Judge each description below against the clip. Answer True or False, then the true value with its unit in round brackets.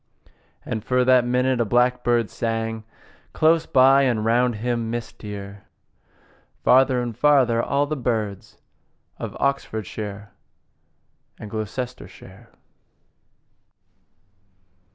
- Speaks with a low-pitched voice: True (120 Hz)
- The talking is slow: True (90 wpm)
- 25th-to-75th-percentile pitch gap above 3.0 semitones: False (2.7 semitones)